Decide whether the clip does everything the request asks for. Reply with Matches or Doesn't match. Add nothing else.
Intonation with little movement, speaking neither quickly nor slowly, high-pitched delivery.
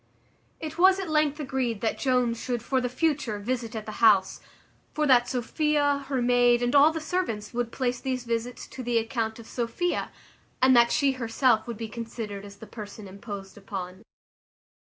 Doesn't match